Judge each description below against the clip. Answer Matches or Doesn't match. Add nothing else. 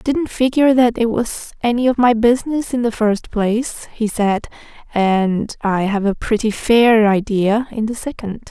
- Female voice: Matches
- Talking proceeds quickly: Doesn't match